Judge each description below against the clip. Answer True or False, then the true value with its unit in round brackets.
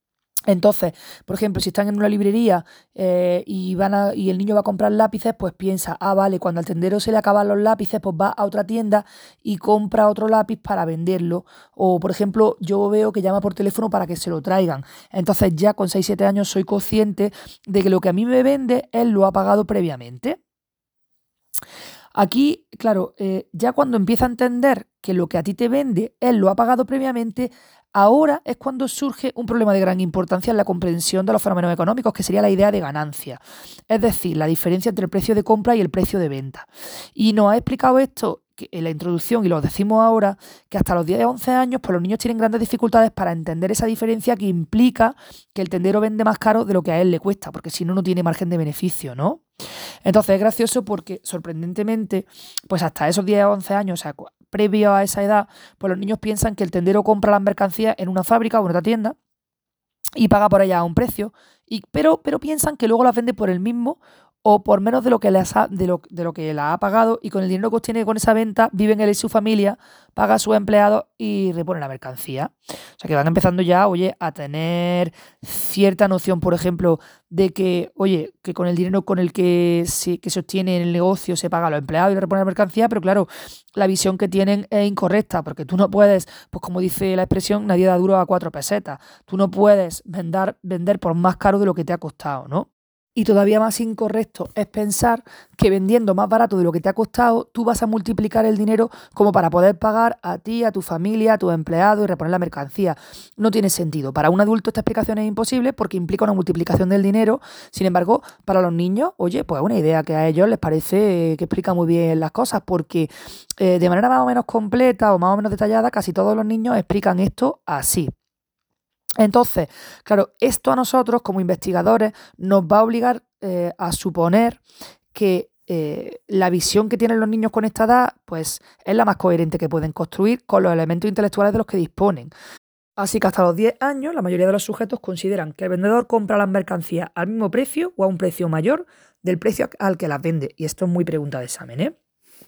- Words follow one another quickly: True (225 wpm)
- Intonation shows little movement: False (3.6 semitones)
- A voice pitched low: False (200 Hz)